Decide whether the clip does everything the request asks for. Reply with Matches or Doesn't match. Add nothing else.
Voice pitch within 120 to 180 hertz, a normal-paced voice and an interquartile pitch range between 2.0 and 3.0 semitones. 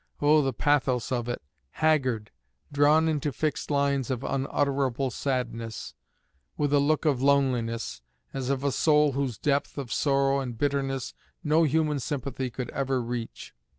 Matches